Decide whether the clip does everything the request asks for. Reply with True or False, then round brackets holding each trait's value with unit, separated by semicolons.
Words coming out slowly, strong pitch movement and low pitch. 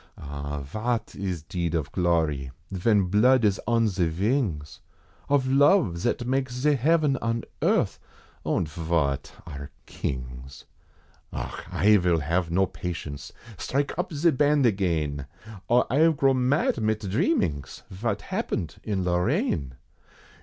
True (130 wpm; 8.1 semitones; 95 Hz)